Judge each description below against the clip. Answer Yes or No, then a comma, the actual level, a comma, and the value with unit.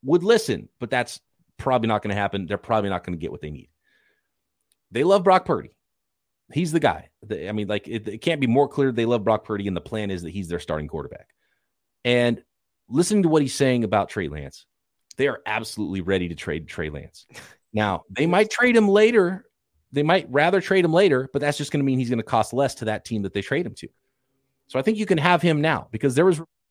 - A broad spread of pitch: Yes, wide, 8.0 semitones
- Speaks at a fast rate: Yes, fast, 240 wpm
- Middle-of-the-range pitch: No, low, 120 Hz